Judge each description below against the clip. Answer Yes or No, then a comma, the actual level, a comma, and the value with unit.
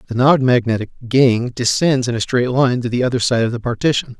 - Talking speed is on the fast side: Yes, fast, 230 wpm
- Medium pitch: No, low, 125 Hz